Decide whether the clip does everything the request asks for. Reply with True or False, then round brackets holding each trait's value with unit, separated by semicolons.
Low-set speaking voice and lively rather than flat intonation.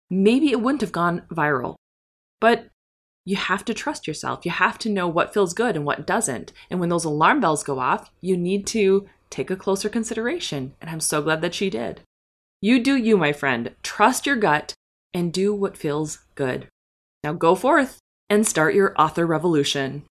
False (180 Hz; 5.8 semitones)